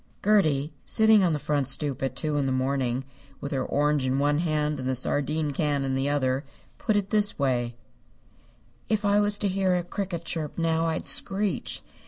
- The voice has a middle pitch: Yes, medium, 150 Hz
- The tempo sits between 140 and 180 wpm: No, average, 195 wpm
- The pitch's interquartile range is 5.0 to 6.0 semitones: Yes, wide, 5.4 semitones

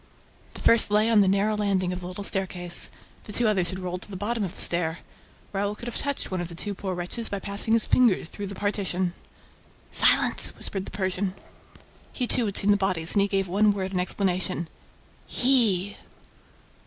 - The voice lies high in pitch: Yes, high, 195 Hz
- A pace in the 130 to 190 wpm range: No, fast, 205 wpm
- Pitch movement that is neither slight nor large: No, narrow, 2.3 semitones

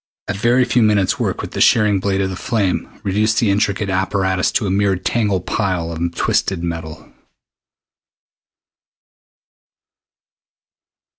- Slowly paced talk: Yes, slow, 125 wpm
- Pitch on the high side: No, low, 100 Hz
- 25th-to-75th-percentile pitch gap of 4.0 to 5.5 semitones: No, narrow, 2.4 semitones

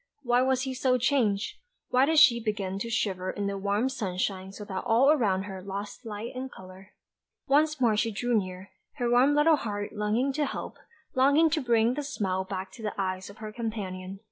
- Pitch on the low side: No, high, 220 Hz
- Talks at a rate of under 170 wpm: No, average, 200 wpm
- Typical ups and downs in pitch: Yes, average, 4.8 semitones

